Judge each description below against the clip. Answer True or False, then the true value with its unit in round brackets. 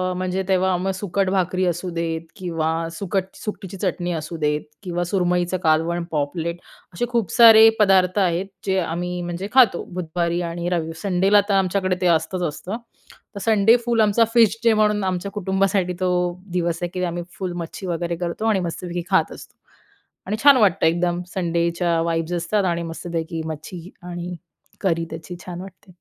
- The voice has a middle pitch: True (180 Hz)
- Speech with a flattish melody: True (2.2 semitones)